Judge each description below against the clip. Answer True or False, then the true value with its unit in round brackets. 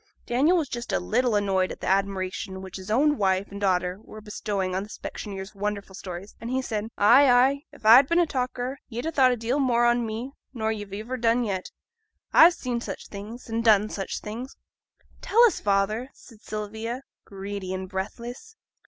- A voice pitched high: True (220 Hz)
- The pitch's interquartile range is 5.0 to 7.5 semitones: False (4.0 semitones)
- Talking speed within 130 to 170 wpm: False (195 wpm)